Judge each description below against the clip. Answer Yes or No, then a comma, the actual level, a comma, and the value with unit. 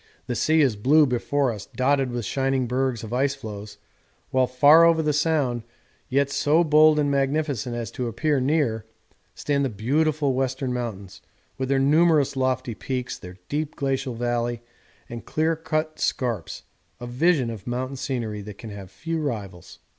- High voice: No, low, 130 Hz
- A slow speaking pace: No, average, 165 wpm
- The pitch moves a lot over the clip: No, average, 3.7 semitones